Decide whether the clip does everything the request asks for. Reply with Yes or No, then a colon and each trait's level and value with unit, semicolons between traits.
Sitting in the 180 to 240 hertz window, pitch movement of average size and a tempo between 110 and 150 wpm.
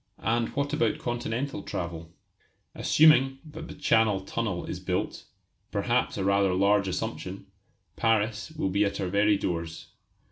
No: low, 105 Hz; average, 3.7 semitones; average, 140 wpm